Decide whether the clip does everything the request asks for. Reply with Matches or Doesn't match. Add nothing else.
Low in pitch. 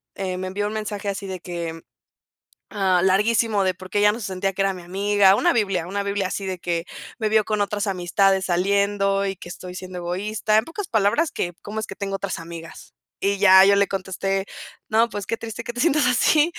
Doesn't match